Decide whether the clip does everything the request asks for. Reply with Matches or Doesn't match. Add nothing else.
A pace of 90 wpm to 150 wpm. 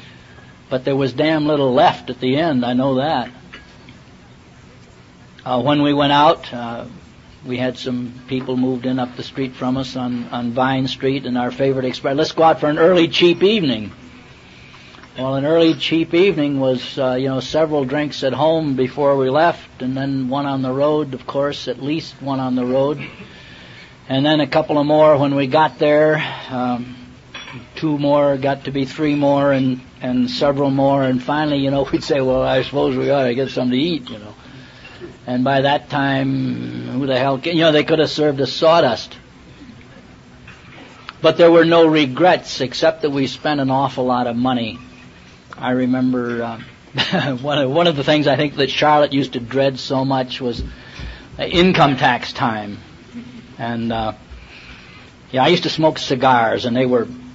Doesn't match